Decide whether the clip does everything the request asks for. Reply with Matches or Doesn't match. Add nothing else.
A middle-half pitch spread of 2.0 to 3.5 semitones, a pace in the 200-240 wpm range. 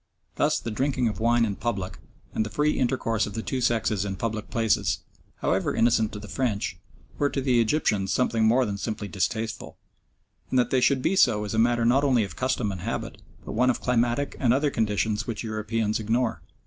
Matches